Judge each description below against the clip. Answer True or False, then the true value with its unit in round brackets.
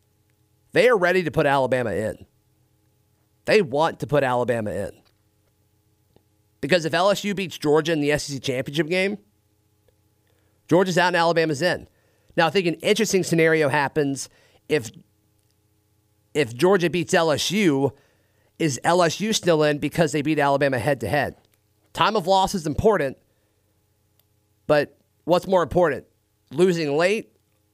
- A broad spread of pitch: True (8.2 semitones)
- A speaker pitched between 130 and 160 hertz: True (140 Hz)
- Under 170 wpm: True (135 wpm)